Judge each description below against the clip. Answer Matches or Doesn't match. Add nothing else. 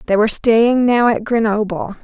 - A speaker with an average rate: Matches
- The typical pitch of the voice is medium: Doesn't match